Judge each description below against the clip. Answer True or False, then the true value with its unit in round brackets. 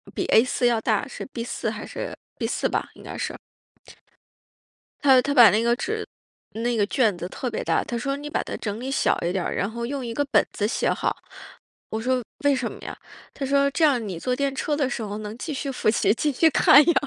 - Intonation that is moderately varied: True (4.0 semitones)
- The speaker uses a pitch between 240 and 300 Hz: True (250 Hz)